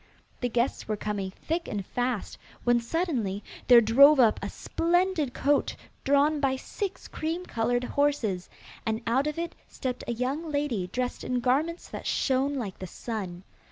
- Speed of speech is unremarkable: Yes, average, 160 wpm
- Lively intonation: No, average, 4.6 semitones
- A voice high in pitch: Yes, very high, 255 Hz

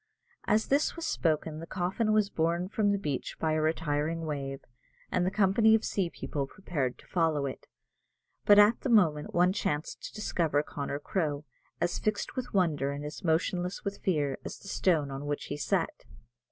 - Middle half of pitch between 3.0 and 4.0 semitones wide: No, average, 5.1 semitones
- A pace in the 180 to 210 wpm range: Yes, average, 185 wpm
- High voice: No, medium, 165 Hz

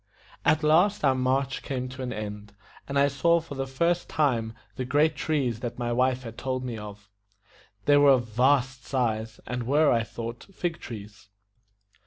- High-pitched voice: No, low, 130 Hz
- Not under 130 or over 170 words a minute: No, average, 180 wpm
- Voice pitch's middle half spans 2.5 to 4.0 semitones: Yes, average, 3.6 semitones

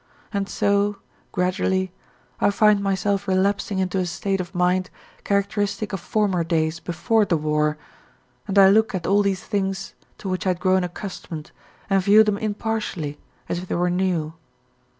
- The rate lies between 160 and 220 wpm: Yes, average, 165 wpm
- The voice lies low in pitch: No, high, 190 Hz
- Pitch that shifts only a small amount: Yes, narrow, 2.2 semitones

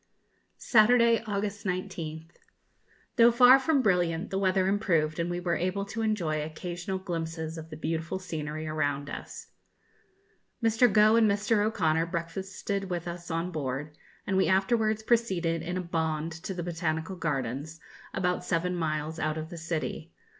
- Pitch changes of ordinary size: Yes, average, 3.8 semitones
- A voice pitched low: No, medium, 175 Hz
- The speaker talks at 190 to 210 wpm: No, average, 155 wpm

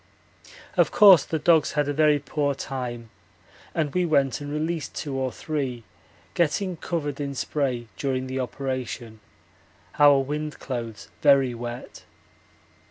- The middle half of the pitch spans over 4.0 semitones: No, average, 2.9 semitones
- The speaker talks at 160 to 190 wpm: No, slow, 135 wpm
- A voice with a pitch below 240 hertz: Yes, medium, 140 Hz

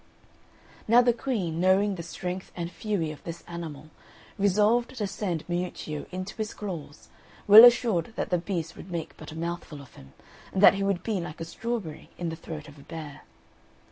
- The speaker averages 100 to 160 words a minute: No, average, 190 wpm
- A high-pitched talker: No, medium, 180 Hz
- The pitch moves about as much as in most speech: Yes, average, 4.1 semitones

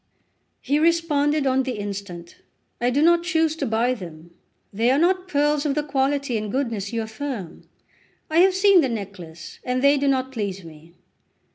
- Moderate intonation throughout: No, wide, 6.4 semitones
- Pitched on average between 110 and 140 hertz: No, very high, 265 Hz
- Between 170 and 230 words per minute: Yes, average, 175 wpm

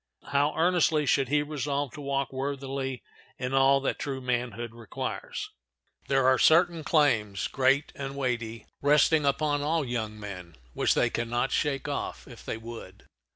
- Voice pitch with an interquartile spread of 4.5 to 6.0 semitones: No, average, 3.2 semitones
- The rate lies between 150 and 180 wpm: Yes, average, 155 wpm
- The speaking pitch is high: No, low, 135 Hz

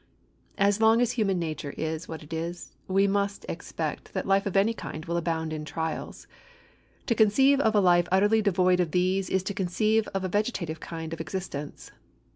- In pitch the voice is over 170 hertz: Yes, medium, 185 Hz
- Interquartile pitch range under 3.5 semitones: No, average, 3.8 semitones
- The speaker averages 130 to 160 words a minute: No, average, 190 wpm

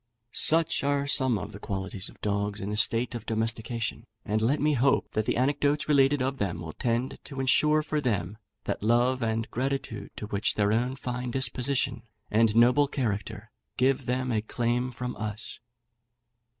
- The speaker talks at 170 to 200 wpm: Yes, average, 175 wpm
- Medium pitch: No, low, 120 Hz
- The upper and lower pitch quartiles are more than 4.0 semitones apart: No, average, 3.5 semitones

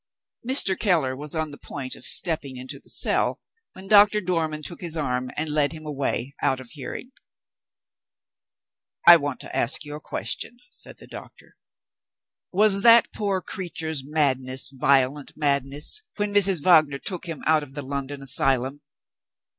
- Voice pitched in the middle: Yes, medium, 150 Hz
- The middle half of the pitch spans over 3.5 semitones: Yes, average, 4.7 semitones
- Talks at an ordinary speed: Yes, average, 155 wpm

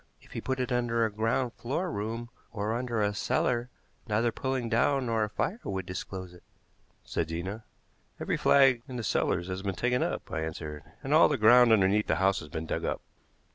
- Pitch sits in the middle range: No, low, 110 Hz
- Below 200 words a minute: No, fast, 205 wpm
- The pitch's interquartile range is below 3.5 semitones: No, average, 4.2 semitones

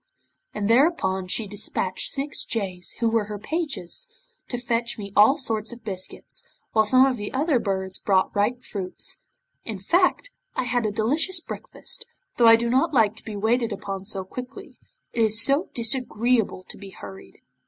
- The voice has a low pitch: No, high, 225 Hz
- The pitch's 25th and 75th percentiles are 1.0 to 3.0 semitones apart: No, average, 4.0 semitones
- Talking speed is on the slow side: No, average, 175 wpm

